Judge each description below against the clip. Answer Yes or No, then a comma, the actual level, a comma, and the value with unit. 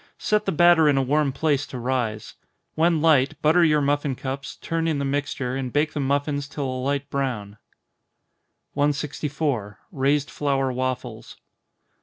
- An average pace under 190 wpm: Yes, average, 155 wpm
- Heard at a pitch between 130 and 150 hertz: Yes, medium, 140 Hz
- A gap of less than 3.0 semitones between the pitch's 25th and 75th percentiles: Yes, narrow, 2.4 semitones